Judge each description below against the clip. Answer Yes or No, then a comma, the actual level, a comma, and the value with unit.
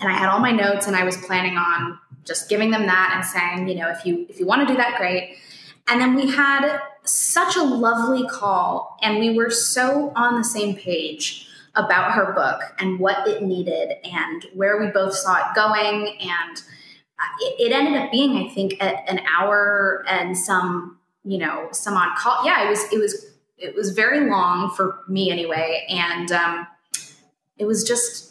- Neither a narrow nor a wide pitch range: Yes, average, 4.7 semitones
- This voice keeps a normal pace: Yes, average, 195 wpm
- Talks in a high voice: Yes, high, 200 Hz